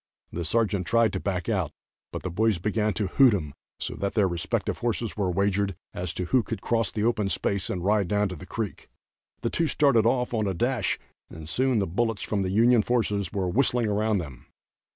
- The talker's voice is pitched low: Yes, low, 105 Hz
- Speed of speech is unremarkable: No, fast, 215 wpm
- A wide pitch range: No, average, 3.6 semitones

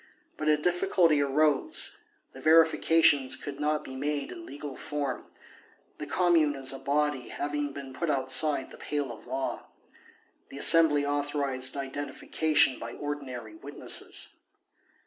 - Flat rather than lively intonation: Yes, narrow, 2.2 semitones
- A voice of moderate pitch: Yes, medium, 145 Hz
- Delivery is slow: Yes, slow, 130 wpm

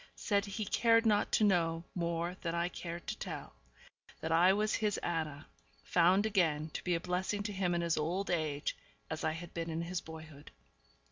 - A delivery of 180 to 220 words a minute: Yes, average, 195 wpm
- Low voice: No, medium, 175 Hz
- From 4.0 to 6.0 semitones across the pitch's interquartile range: No, average, 3.2 semitones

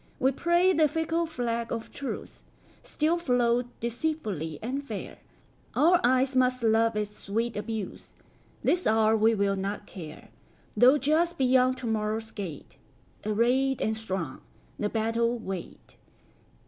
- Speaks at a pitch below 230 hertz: No, high, 235 Hz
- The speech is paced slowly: Yes, slow, 115 wpm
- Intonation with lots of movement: No, average, 4.0 semitones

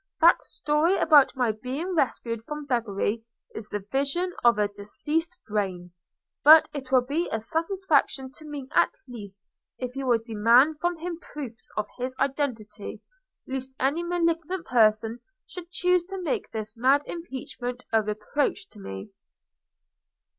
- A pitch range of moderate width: No, wide, 6.1 semitones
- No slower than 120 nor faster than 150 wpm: Yes, average, 145 wpm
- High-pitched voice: Yes, very high, 265 Hz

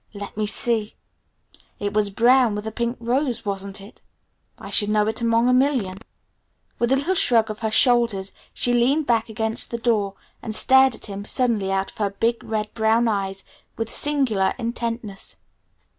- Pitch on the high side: Yes, high, 225 Hz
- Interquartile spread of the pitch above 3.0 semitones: No, average, 2.7 semitones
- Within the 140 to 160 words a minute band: No, average, 175 wpm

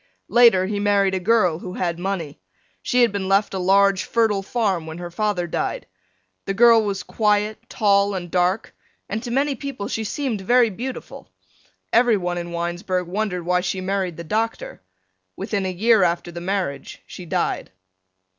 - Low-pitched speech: No, high, 195 Hz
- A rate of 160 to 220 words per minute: Yes, average, 170 wpm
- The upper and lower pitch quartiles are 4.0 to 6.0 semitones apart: No, average, 3.4 semitones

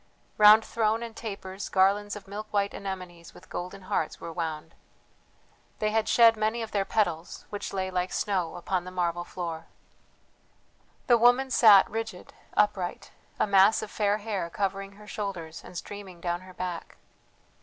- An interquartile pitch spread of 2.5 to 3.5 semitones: Yes, average, 3.0 semitones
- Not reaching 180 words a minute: Yes, average, 160 wpm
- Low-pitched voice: No, high, 195 Hz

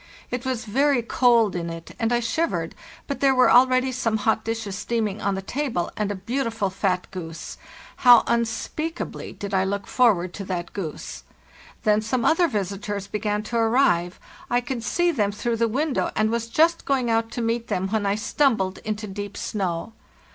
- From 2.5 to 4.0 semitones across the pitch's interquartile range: Yes, average, 3.7 semitones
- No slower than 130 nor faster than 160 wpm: No, average, 185 wpm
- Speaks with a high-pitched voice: Yes, high, 225 Hz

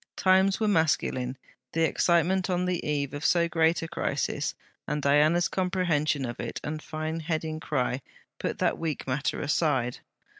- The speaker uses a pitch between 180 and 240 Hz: No, medium, 160 Hz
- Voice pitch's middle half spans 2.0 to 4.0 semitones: Yes, average, 2.9 semitones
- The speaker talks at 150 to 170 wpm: Yes, average, 155 wpm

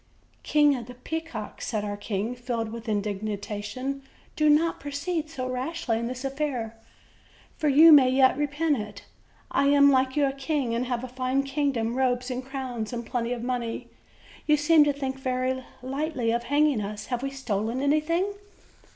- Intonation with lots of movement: No, average, 3.5 semitones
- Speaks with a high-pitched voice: Yes, very high, 260 Hz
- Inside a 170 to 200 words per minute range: Yes, average, 175 wpm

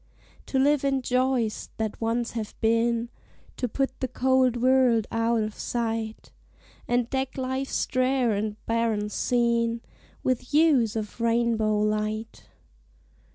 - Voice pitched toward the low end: No, high, 235 Hz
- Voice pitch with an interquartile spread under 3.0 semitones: Yes, narrow, 2.5 semitones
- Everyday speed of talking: No, slow, 125 wpm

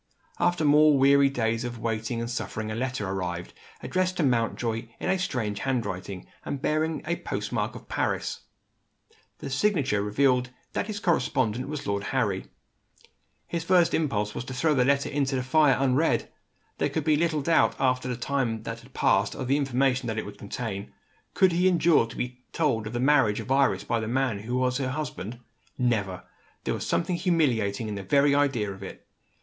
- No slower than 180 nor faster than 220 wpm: Yes, average, 190 wpm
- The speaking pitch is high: No, low, 130 Hz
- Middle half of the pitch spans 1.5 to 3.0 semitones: No, average, 4.6 semitones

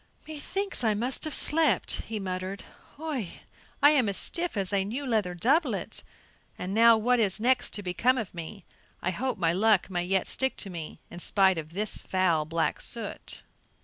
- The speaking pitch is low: No, high, 205 Hz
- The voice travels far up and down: Yes, wide, 5.7 semitones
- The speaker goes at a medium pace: Yes, average, 180 wpm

